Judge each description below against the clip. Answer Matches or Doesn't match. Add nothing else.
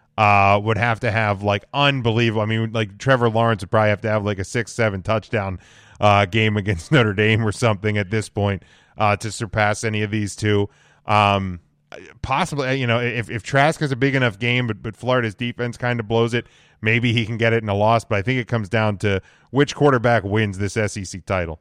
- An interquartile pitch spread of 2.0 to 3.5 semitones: Matches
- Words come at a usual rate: Doesn't match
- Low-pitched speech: Matches